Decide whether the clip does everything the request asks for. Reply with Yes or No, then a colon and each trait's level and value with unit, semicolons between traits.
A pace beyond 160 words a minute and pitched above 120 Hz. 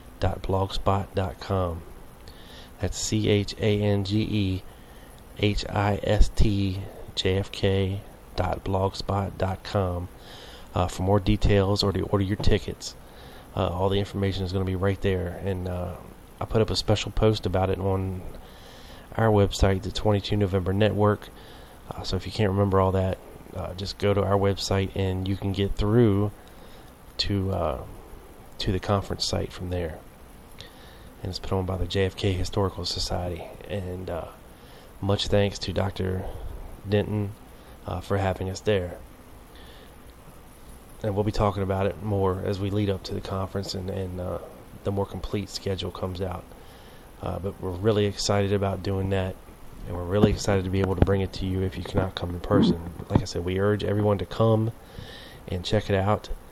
No: average, 175 wpm; very low, 95 Hz